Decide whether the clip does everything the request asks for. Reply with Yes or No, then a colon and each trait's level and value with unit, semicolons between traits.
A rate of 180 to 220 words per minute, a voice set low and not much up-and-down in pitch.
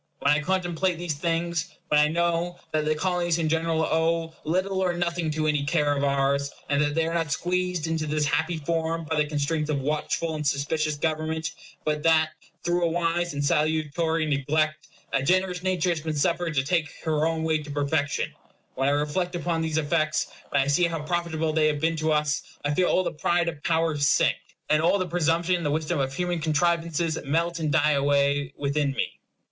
No: fast, 205 wpm; medium, 160 Hz; narrow, 2.2 semitones